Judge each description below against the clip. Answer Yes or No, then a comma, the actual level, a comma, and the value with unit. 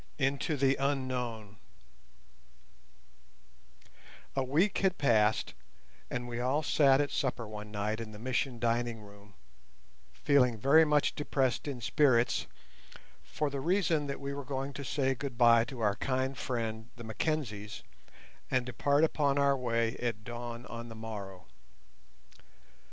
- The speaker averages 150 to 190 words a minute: No, slow, 135 wpm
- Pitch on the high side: No, low, 125 Hz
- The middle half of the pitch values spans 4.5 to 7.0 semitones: No, average, 3.6 semitones